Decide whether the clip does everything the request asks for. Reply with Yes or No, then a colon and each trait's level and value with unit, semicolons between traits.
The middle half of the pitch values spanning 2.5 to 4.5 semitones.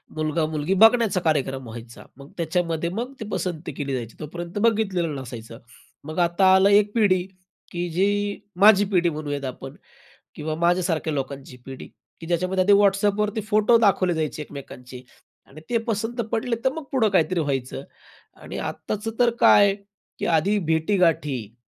No: wide, 5.4 semitones